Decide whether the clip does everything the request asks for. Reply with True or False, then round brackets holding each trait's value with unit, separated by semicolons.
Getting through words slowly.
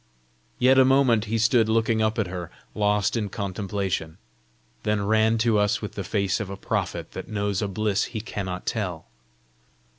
False (175 wpm)